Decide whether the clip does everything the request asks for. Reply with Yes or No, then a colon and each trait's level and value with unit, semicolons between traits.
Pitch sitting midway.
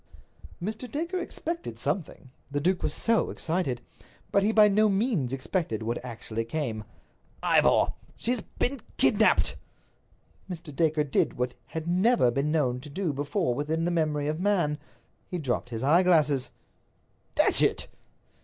Yes: medium, 160 Hz